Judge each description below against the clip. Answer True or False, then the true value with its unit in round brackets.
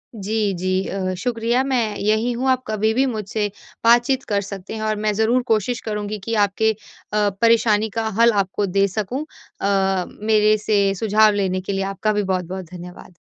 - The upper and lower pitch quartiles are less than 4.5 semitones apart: True (2.5 semitones)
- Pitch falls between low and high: False (215 Hz)